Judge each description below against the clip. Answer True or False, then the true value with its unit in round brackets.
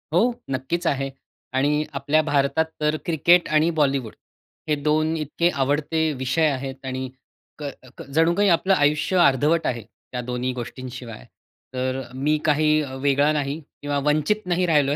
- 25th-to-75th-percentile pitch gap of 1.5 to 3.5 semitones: True (2.9 semitones)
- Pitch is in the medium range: True (145 Hz)